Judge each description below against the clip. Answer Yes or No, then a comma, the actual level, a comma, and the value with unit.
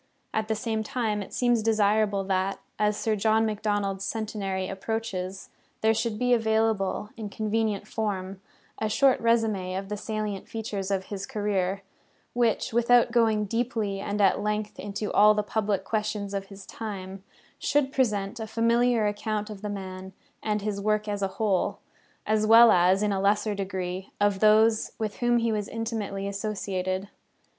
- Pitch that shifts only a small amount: Yes, narrow, 2.0 semitones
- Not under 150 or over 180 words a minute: Yes, average, 165 wpm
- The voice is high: Yes, high, 210 Hz